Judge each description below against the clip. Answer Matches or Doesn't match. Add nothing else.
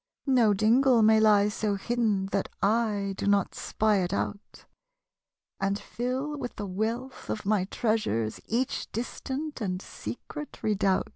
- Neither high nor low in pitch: Doesn't match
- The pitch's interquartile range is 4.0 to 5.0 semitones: Doesn't match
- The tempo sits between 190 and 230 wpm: Doesn't match